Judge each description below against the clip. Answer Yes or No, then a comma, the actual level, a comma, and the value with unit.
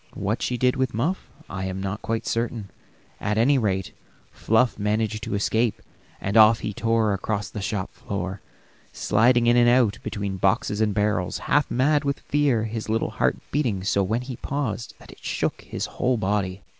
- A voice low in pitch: Yes, low, 110 Hz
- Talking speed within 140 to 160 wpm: No, average, 180 wpm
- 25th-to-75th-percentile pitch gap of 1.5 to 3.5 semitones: Yes, average, 3.2 semitones